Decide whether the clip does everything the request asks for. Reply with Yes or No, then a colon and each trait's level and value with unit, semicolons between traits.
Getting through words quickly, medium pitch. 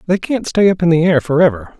Yes: fast, 265 wpm; medium, 170 Hz